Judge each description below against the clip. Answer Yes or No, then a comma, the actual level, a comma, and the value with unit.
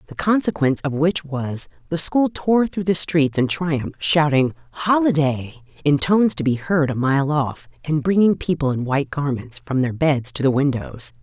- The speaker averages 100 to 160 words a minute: No, average, 185 wpm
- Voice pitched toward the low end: No, medium, 150 Hz